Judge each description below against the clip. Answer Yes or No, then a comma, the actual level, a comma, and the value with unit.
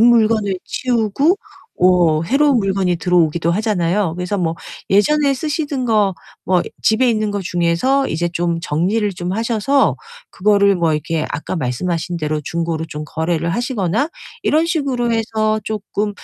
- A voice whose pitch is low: No, high, 200 Hz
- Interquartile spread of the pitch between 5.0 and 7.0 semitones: Yes, average, 5.3 semitones